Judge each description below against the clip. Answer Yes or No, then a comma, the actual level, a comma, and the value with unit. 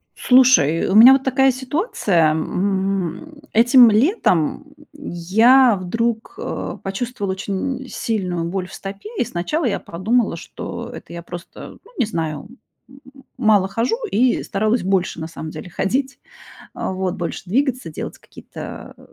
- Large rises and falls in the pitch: Yes, wide, 6.2 semitones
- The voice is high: Yes, high, 210 Hz